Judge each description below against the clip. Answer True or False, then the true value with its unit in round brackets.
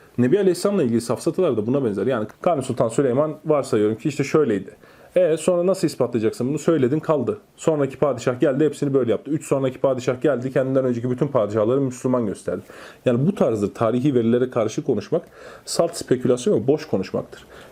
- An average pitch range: True (3.8 semitones)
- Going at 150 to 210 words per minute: True (170 wpm)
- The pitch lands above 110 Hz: True (140 Hz)